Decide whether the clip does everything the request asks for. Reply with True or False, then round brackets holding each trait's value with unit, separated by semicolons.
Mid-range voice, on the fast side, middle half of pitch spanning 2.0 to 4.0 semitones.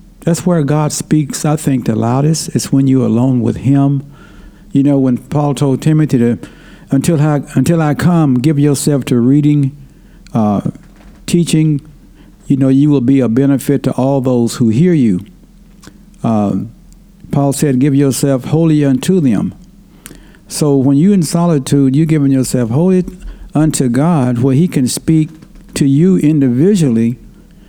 False (145 Hz; 155 wpm; 3.5 semitones)